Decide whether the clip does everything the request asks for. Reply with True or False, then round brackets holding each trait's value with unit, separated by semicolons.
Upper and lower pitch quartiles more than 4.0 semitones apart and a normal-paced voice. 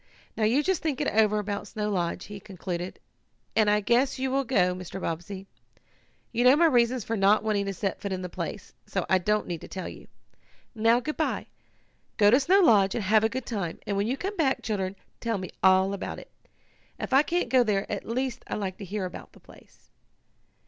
False (4.5 semitones; 220 wpm)